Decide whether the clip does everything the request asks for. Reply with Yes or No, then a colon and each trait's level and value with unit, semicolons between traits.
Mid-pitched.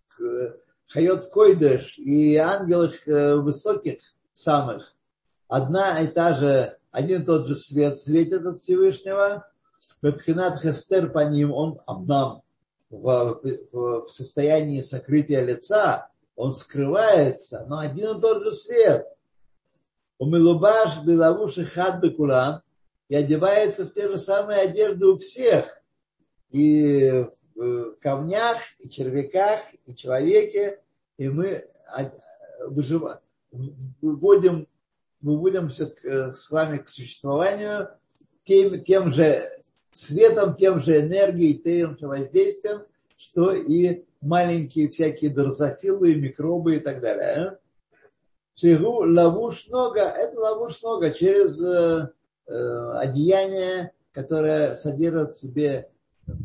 Yes: medium, 165 Hz